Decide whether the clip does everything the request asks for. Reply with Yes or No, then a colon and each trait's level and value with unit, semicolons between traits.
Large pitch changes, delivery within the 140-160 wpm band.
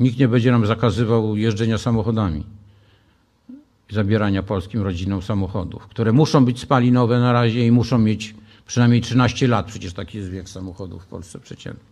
No: average, 3.1 semitones; average, 155 wpm